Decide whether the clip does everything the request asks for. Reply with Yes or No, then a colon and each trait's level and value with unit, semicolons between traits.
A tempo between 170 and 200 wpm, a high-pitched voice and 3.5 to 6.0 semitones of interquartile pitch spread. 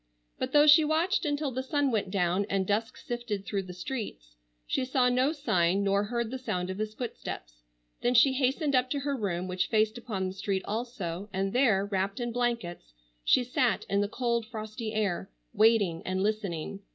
Yes: average, 190 wpm; high, 215 Hz; average, 4.7 semitones